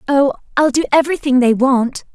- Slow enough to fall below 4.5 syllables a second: No, 5.7 syllables/s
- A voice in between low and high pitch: No, very high, 270 Hz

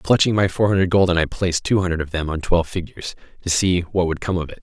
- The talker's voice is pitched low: Yes, very low, 90 Hz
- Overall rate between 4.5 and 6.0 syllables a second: No, 6.7 syllables/s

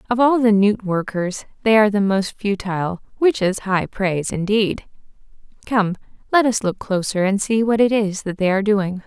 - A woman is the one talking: Yes, female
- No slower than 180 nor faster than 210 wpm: Yes, average, 190 wpm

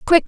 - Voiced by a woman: Yes, female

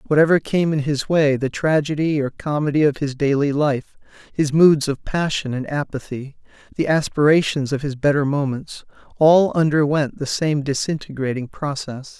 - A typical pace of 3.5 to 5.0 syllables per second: Yes, 4.9 syllables/s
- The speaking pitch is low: No, medium, 145 Hz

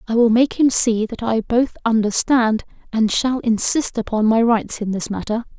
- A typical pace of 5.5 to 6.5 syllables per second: No, 4.6 syllables/s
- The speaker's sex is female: Yes, female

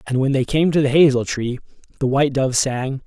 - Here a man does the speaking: Yes, male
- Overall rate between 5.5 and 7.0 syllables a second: Yes, 5.6 syllables/s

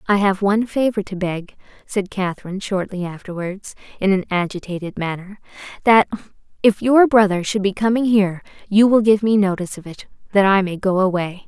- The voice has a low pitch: No, high, 195 Hz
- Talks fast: No, average, 180 wpm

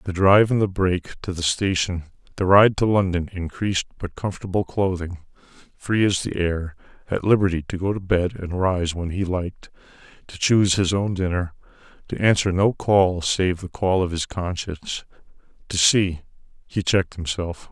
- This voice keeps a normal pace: Yes, average, 175 wpm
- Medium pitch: No, very low, 90 Hz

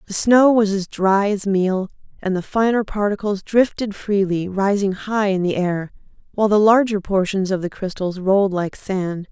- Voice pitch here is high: Yes, high, 200 Hz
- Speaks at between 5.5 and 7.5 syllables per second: No, 4.6 syllables/s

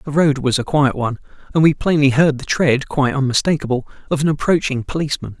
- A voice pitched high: No, medium, 140 Hz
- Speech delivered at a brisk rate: No, average, 180 wpm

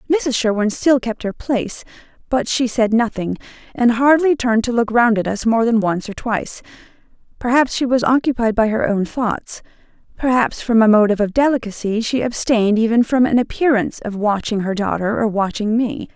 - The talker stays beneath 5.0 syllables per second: No, 5.4 syllables/s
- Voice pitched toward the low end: No, high, 230 Hz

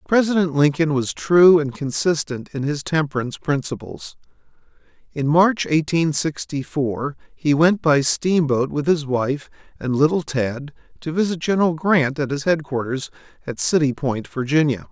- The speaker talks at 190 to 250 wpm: No, average, 145 wpm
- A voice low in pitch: No, medium, 150 Hz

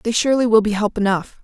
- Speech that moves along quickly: Yes, fast, 250 wpm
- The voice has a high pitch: Yes, high, 215 Hz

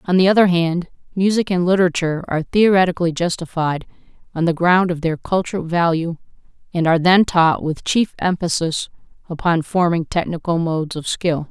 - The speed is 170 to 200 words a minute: No, average, 155 wpm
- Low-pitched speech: No, medium, 170 Hz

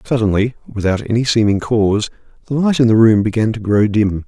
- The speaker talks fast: No, average, 195 wpm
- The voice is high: No, low, 110 Hz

